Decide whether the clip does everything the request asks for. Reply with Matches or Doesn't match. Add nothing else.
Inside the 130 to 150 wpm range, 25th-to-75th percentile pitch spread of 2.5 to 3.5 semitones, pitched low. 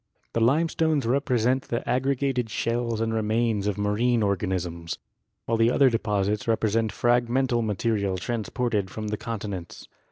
Matches